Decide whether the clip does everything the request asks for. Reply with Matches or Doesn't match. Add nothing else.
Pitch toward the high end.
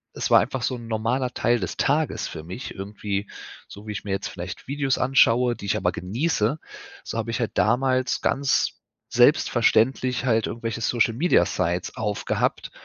Doesn't match